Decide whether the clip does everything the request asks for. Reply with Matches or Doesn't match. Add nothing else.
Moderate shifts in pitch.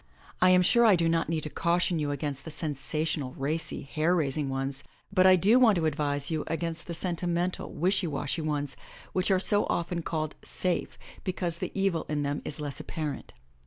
Matches